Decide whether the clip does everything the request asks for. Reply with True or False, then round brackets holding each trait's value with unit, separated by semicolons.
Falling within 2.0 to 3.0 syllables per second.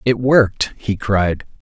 False (3.7 syllables/s)